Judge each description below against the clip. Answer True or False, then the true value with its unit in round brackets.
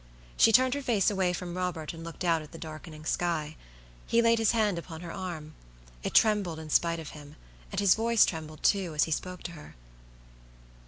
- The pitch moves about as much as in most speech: True (4.1 semitones)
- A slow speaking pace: False (205 wpm)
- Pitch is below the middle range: False (175 Hz)